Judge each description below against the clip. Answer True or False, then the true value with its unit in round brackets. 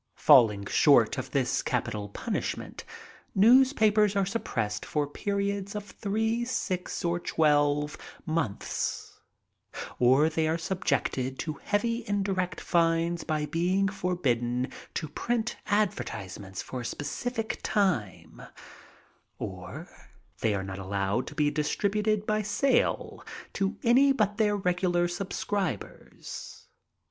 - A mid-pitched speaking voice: True (175 Hz)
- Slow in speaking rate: True (115 wpm)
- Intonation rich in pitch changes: True (6.0 semitones)